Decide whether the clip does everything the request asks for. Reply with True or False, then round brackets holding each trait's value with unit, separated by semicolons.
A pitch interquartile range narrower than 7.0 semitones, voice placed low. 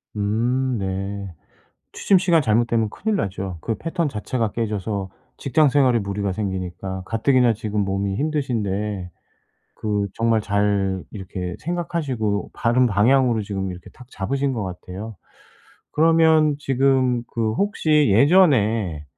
True (5.3 semitones; 110 Hz)